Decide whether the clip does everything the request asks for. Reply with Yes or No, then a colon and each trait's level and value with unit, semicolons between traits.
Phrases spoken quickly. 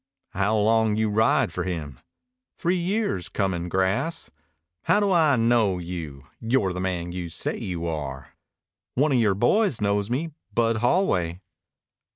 No: average, 150 wpm